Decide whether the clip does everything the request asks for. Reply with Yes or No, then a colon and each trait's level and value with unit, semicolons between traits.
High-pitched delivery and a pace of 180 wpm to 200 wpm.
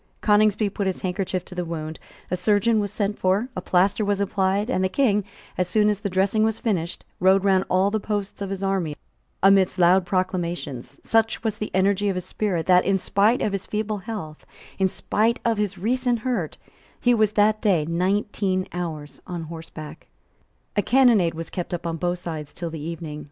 Yes: high, 195 Hz; average, 195 wpm